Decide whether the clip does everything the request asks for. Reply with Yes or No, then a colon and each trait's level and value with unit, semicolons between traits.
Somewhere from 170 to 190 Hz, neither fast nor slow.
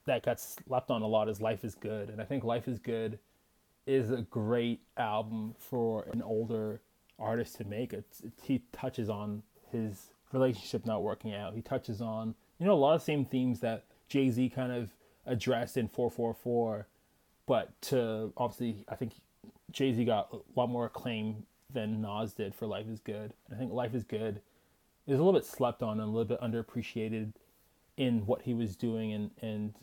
No: low, 115 Hz; average, 195 wpm